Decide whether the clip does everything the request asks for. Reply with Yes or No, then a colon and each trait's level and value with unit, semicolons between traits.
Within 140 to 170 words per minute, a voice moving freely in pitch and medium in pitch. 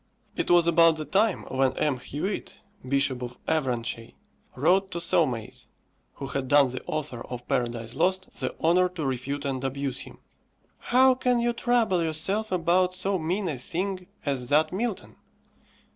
Yes: average, 160 wpm; wide, 5.8 semitones; medium, 155 Hz